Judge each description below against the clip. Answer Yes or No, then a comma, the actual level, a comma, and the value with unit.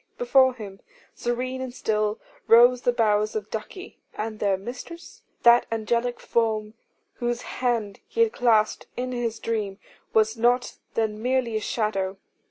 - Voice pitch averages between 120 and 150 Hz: No, high, 230 Hz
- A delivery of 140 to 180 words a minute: Yes, average, 145 wpm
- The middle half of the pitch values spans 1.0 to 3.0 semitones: Yes, narrow, 2.5 semitones